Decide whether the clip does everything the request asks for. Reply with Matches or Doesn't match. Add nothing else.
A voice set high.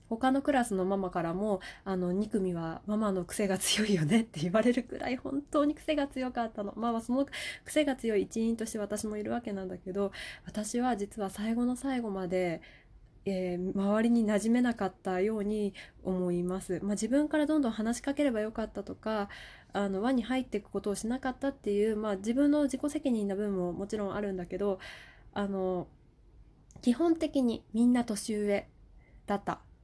Matches